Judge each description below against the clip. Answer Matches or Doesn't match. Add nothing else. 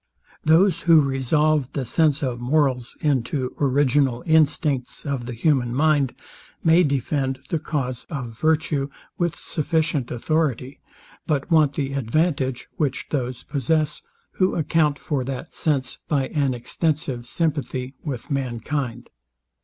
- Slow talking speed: Matches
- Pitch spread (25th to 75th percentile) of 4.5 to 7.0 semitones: Doesn't match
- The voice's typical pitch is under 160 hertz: Matches